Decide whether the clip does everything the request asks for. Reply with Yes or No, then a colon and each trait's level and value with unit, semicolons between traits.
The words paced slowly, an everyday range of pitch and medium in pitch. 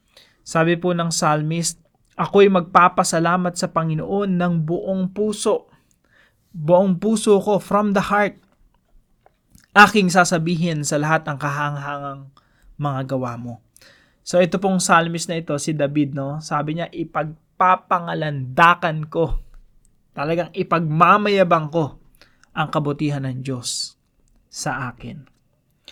Yes: slow, 110 wpm; average, 3.8 semitones; medium, 165 Hz